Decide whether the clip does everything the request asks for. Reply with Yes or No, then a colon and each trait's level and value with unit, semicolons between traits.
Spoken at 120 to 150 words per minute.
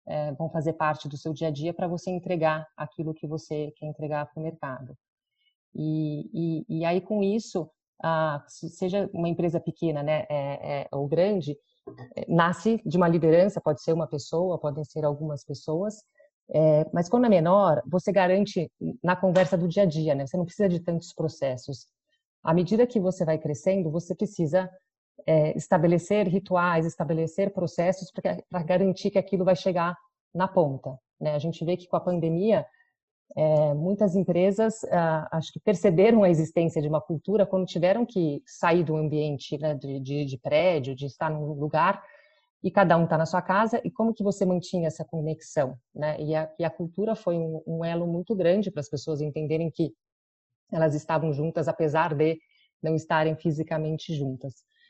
No: average, 180 wpm